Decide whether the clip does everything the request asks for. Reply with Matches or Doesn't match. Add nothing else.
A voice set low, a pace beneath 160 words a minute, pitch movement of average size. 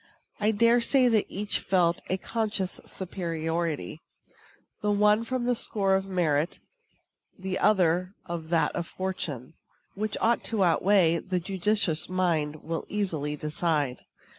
Doesn't match